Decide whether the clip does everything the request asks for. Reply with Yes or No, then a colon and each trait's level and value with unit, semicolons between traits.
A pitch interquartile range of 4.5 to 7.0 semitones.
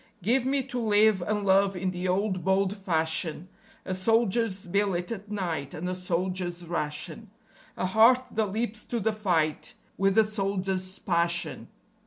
No: average, 3.1 semitones